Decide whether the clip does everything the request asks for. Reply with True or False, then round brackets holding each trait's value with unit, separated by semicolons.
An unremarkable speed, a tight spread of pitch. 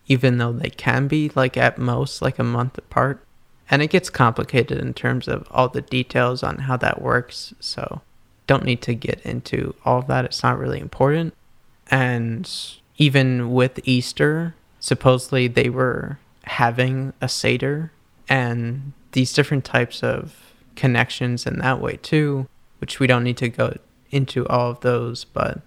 True (165 wpm; 2.0 semitones)